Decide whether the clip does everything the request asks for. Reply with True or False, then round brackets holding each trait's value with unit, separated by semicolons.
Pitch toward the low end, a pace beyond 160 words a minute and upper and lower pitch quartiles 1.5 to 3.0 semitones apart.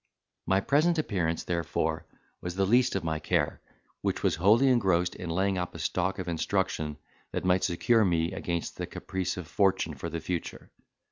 True (90 Hz; 180 wpm; 2.7 semitones)